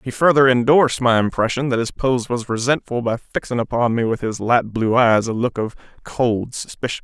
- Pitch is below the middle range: Yes, low, 120 Hz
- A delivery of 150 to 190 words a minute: No, fast, 205 wpm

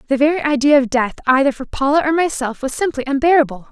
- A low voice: No, very high, 275 Hz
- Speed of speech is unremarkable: No, fast, 210 wpm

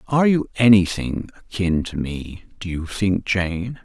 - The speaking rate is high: No, average, 155 wpm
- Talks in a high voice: No, very low, 95 Hz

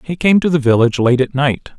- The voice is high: No, medium, 140 Hz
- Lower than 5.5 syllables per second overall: No, 6.1 syllables/s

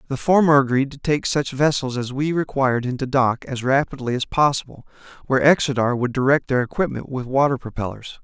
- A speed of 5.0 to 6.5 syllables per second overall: Yes, 5.7 syllables/s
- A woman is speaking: No, male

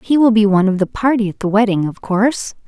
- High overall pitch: Yes, high, 210 Hz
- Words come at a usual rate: No, fast, 270 wpm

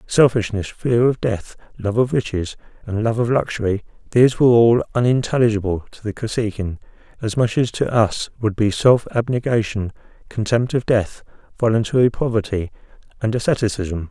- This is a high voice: No, low, 110 Hz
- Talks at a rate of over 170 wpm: No, average, 145 wpm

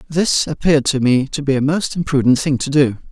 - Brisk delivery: Yes, fast, 230 wpm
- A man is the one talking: Yes, male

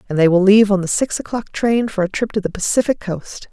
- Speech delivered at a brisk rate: Yes, fast, 275 wpm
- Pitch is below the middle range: No, high, 205 Hz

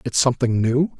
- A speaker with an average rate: Yes, average, 180 wpm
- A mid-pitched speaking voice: No, low, 125 Hz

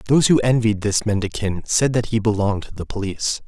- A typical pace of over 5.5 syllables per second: Yes, 5.9 syllables/s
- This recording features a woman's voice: No, male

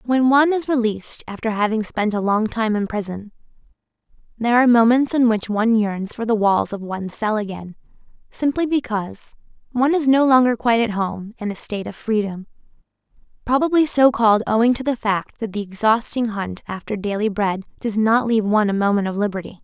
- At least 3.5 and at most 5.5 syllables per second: No, 5.8 syllables/s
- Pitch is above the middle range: Yes, high, 220 Hz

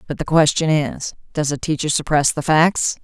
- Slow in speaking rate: No, average, 200 wpm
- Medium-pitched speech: Yes, medium, 150 Hz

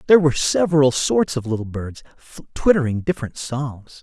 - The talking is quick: No, average, 150 wpm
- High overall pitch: No, low, 135 Hz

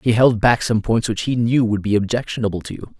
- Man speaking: Yes, male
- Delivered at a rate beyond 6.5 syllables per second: No, 5.8 syllables/s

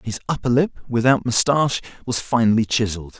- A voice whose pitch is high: No, low, 120 Hz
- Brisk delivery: No, average, 150 wpm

